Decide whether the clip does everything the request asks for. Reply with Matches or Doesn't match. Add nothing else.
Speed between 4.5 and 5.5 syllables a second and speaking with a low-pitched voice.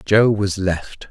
Doesn't match